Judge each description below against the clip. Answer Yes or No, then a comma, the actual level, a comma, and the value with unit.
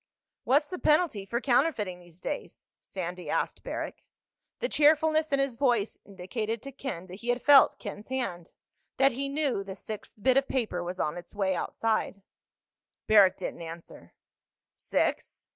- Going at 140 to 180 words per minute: Yes, average, 155 wpm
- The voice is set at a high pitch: Yes, high, 225 Hz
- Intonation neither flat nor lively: No, wide, 6.7 semitones